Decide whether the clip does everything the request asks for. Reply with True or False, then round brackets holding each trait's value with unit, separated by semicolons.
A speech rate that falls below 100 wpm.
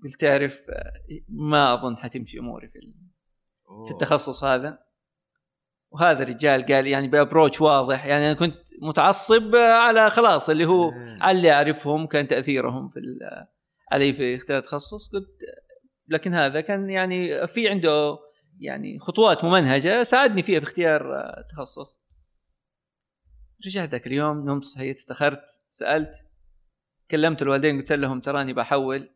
False (125 wpm)